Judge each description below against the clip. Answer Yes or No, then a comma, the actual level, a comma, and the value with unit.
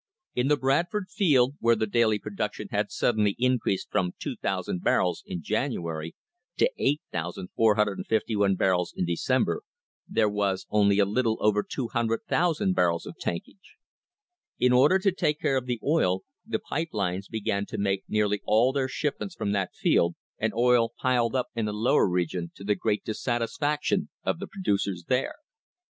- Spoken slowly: No, average, 155 wpm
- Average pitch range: Yes, average, 4.6 semitones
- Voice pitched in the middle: No, low, 110 Hz